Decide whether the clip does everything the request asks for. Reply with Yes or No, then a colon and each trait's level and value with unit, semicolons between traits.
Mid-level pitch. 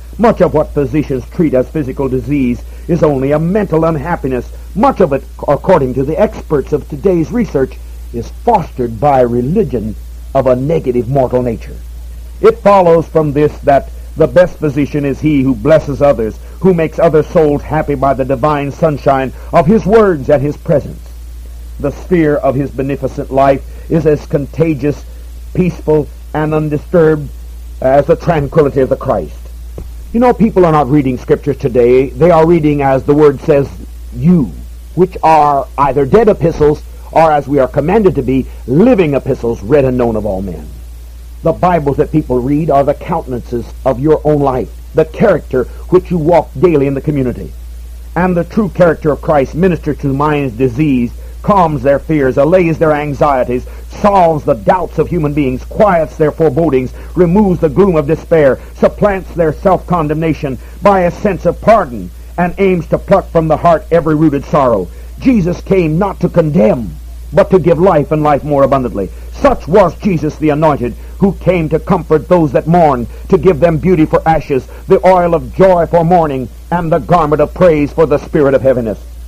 Yes: medium, 150 Hz